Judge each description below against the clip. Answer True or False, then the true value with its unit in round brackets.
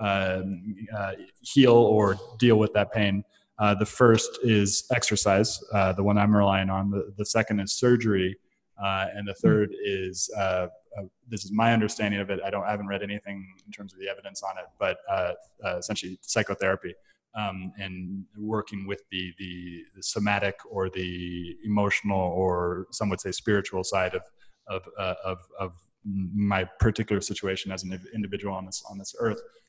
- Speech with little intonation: True (1.9 semitones)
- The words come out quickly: False (180 wpm)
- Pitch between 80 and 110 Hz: True (100 Hz)